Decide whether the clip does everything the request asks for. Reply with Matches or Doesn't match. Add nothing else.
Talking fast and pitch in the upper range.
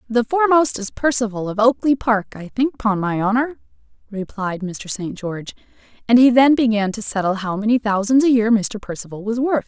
Doesn't match